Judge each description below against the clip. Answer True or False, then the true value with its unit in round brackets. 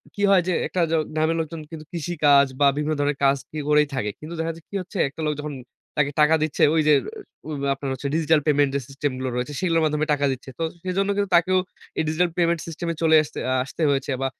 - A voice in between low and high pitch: True (155 Hz)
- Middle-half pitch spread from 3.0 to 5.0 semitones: False (2.6 semitones)